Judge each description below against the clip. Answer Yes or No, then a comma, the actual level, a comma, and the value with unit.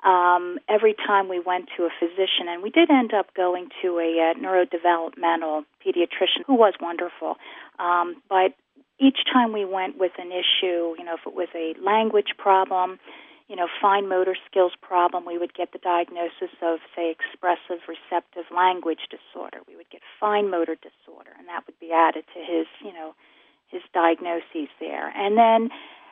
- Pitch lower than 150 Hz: No, medium, 180 Hz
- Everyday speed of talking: Yes, average, 175 wpm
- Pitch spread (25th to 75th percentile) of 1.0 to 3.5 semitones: Yes, average, 2.8 semitones